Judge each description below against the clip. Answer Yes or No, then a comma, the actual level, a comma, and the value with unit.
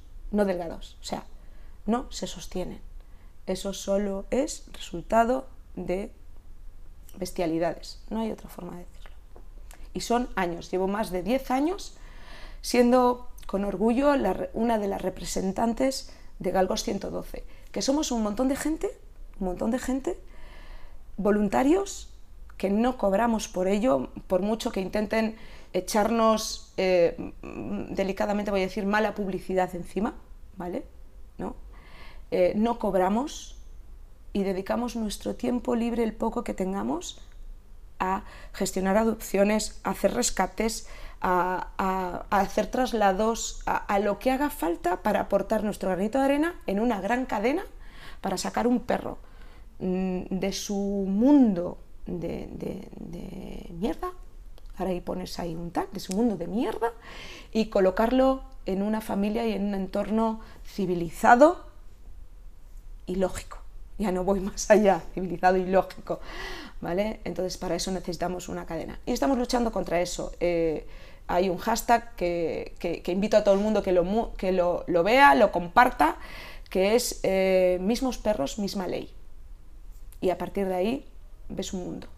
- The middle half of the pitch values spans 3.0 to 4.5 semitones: Yes, average, 4.1 semitones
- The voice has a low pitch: No, high, 200 Hz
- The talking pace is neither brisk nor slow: Yes, average, 140 wpm